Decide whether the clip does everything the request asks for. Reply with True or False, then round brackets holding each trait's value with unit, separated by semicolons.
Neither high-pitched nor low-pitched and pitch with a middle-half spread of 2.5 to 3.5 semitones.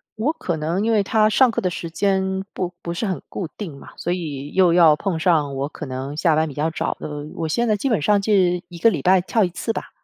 False (180 Hz; 4.2 semitones)